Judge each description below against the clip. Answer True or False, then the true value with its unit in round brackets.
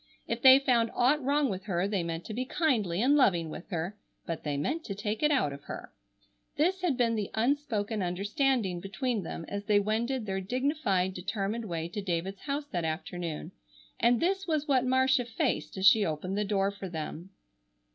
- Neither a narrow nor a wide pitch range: False (6.0 semitones)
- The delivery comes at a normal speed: True (195 wpm)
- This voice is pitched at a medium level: False (210 Hz)